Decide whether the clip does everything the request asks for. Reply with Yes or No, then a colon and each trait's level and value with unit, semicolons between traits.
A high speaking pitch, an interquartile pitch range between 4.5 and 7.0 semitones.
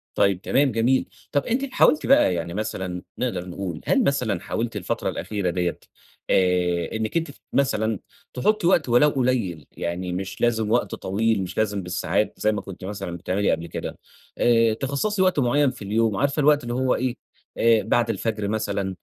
No: low, 110 Hz; wide, 5.4 semitones